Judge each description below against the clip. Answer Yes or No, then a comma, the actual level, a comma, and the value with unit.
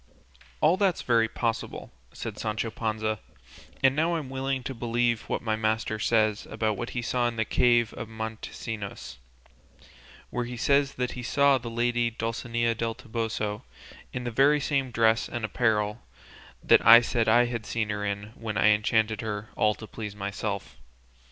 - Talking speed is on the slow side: No, average, 165 wpm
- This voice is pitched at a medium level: No, low, 115 Hz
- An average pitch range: No, narrow, 2.0 semitones